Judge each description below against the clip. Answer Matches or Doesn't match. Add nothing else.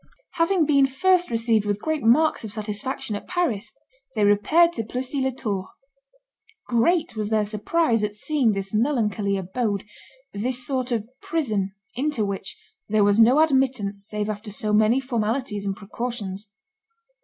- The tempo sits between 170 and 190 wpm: Doesn't match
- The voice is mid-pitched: Doesn't match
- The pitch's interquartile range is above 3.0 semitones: Matches